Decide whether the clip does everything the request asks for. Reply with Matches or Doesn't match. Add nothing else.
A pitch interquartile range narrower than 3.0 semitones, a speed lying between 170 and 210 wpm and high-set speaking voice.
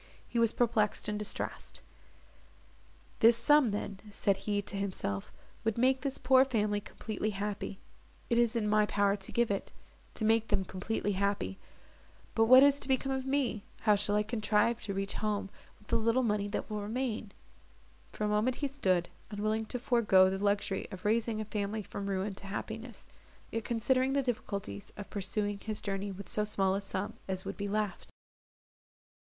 Matches